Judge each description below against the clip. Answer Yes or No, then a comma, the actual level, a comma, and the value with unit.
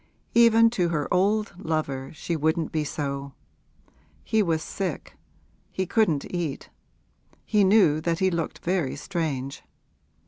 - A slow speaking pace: Yes, slow, 130 wpm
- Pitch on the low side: No, medium, 170 Hz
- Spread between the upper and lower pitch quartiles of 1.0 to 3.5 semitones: No, average, 4.4 semitones